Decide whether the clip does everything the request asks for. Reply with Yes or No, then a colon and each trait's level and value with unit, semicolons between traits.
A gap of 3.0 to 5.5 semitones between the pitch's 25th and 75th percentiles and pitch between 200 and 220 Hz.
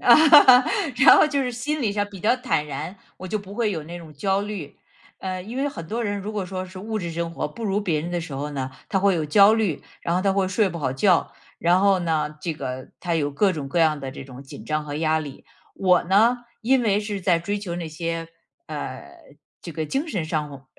No: average, 5.0 semitones; medium, 185 Hz